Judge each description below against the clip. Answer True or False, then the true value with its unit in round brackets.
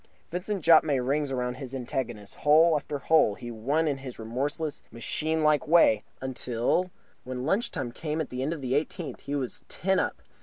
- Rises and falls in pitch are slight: False (4.0 semitones)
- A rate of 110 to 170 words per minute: False (190 wpm)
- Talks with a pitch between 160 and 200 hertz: False (140 Hz)